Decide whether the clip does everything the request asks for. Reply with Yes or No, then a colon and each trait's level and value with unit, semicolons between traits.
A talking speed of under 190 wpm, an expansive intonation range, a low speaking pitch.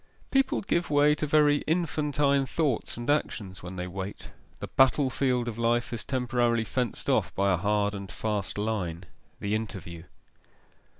Yes: average, 160 wpm; wide, 6.2 semitones; low, 120 Hz